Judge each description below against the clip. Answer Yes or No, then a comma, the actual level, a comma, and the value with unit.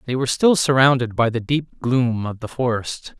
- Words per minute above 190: Yes, fast, 205 wpm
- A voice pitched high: No, low, 125 Hz